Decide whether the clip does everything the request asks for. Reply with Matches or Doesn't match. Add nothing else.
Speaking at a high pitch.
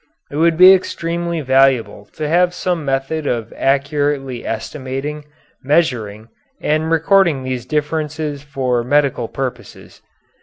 Doesn't match